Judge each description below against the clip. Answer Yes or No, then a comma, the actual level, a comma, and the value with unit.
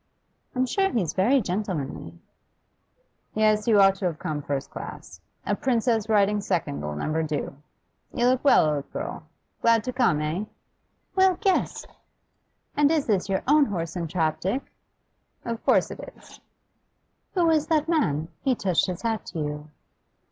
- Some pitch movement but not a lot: No, wide, 8.2 semitones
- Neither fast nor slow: Yes, average, 155 wpm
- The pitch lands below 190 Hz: No, high, 205 Hz